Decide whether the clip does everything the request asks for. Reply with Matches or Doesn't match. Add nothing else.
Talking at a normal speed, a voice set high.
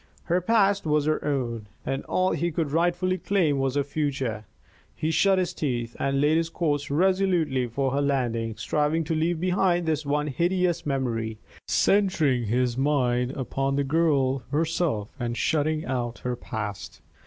Doesn't match